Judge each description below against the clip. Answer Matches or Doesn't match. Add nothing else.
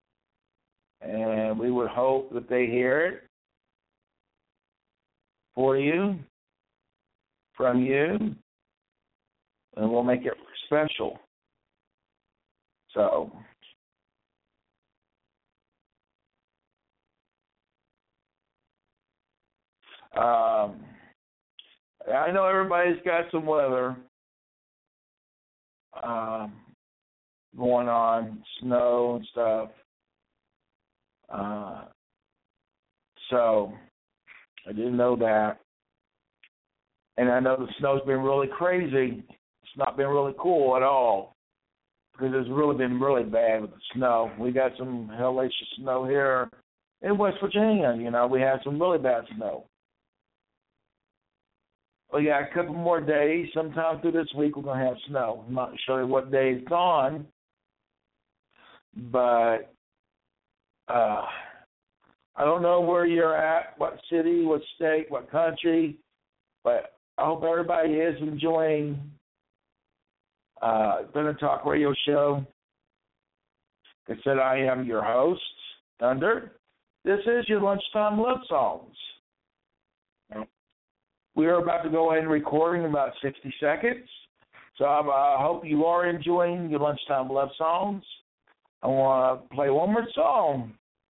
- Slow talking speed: Matches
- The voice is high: Doesn't match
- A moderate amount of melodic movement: Matches